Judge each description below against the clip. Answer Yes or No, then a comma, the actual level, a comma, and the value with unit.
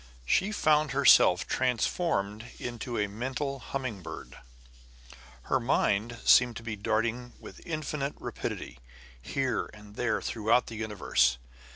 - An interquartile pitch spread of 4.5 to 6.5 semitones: No, average, 4.1 semitones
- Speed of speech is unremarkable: No, slow, 125 wpm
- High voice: No, low, 120 Hz